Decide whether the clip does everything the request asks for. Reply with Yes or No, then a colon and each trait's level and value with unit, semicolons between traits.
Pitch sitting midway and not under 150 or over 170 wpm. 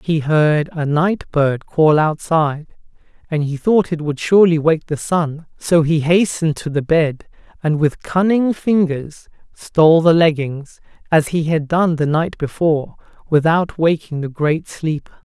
Yes: medium, 160 Hz; average, 160 wpm